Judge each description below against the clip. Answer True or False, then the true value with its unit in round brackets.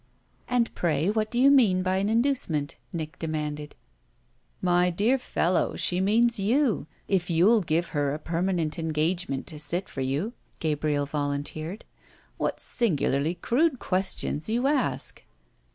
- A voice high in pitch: False (175 Hz)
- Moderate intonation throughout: False (6.1 semitones)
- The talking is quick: False (135 wpm)